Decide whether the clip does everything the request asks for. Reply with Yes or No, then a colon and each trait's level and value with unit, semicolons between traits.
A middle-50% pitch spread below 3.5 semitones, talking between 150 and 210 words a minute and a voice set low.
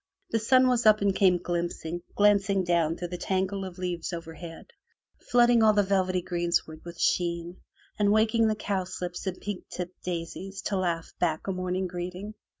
No: average, 2.7 semitones; average, 170 wpm; medium, 185 Hz